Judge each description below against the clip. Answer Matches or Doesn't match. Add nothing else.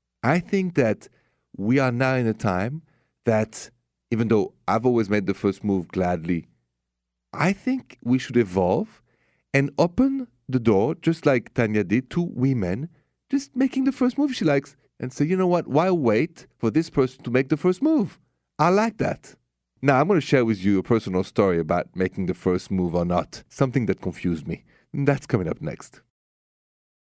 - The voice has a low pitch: Matches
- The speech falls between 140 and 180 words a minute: Doesn't match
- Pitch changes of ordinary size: Doesn't match